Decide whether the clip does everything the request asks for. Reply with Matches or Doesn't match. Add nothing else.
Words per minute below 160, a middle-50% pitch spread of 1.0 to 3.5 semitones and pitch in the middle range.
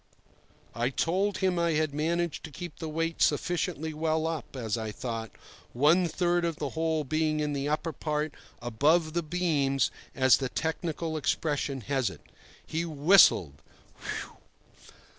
Matches